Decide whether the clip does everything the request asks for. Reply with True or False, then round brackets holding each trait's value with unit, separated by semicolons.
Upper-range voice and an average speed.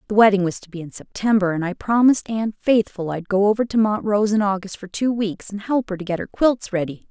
False (205 Hz; 255 wpm)